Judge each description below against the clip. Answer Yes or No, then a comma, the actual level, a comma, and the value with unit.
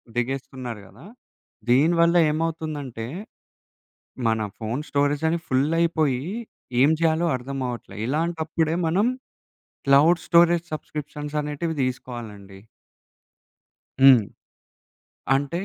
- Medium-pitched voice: Yes, medium, 145 Hz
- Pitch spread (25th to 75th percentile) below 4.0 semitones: No, average, 4.3 semitones